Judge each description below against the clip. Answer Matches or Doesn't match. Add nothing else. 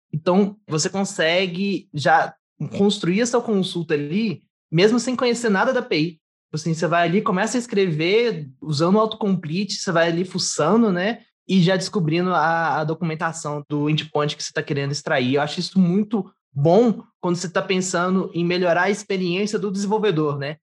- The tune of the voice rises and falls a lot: Doesn't match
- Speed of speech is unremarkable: Matches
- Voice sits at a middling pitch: Matches